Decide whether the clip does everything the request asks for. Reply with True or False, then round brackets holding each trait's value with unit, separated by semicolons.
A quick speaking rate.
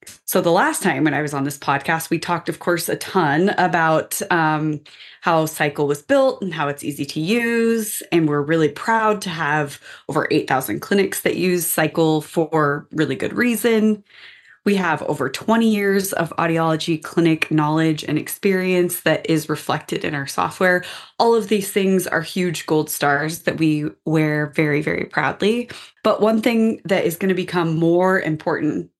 False (175 wpm)